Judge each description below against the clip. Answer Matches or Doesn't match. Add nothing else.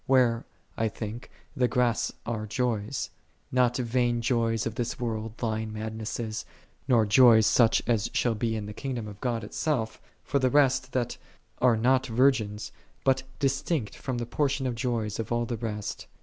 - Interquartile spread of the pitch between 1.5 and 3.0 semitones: Matches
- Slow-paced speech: Doesn't match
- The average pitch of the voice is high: Doesn't match